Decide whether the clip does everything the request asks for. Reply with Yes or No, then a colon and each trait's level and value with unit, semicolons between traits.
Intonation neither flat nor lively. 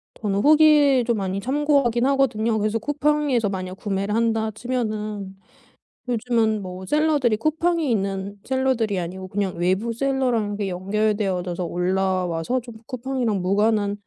Yes: average, 4.9 semitones